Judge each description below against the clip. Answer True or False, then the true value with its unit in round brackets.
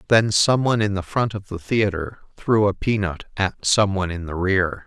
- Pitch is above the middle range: False (100 Hz)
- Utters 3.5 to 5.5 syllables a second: True (5.0 syllables/s)